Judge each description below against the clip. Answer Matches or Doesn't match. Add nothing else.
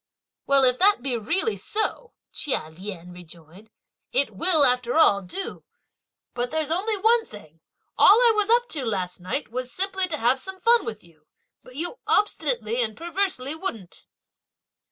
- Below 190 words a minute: Matches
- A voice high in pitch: Matches